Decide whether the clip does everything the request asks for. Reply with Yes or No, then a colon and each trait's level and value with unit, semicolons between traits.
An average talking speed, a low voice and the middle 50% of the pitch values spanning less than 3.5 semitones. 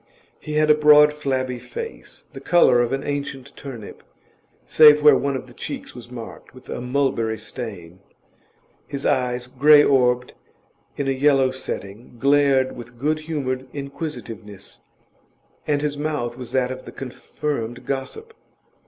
Yes: average, 145 wpm; low, 130 Hz; average, 3.1 semitones